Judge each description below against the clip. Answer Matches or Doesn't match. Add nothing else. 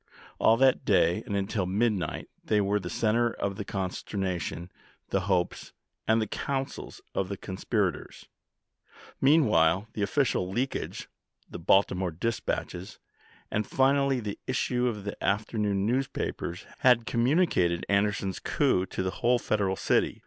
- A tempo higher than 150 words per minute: Doesn't match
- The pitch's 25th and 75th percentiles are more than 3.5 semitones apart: Matches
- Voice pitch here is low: Matches